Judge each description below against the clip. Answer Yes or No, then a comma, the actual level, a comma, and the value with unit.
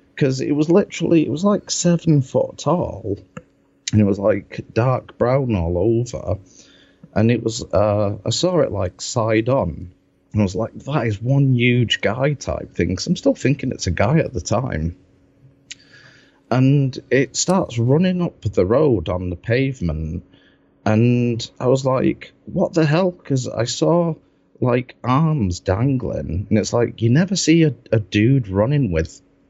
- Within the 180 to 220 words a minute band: No, average, 170 wpm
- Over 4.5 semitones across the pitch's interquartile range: Yes, wide, 5.4 semitones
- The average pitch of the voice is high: No, low, 120 Hz